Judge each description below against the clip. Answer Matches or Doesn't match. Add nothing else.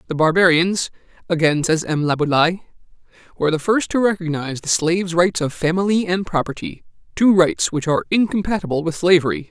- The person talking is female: Doesn't match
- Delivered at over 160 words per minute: Doesn't match